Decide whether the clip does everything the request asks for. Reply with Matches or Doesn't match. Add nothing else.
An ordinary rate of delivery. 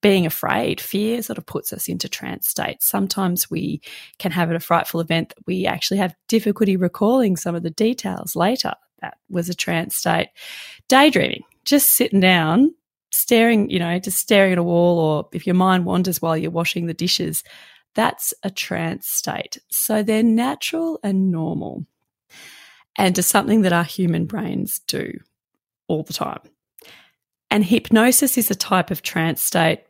Matches